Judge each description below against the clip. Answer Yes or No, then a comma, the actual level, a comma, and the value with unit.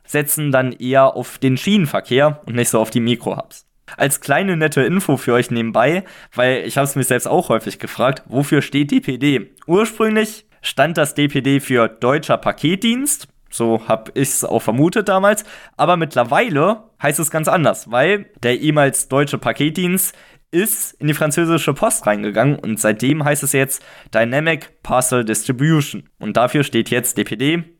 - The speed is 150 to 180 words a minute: Yes, average, 160 wpm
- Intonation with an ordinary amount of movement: Yes, average, 4.6 semitones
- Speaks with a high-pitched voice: No, medium, 140 Hz